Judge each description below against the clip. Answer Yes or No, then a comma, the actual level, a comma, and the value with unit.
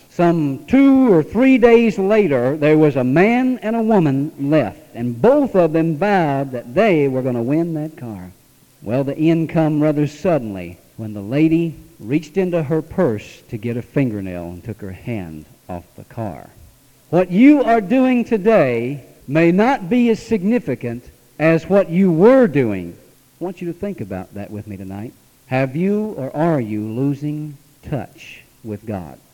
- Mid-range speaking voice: Yes, medium, 150 Hz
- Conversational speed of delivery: Yes, average, 175 wpm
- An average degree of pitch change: No, wide, 7.7 semitones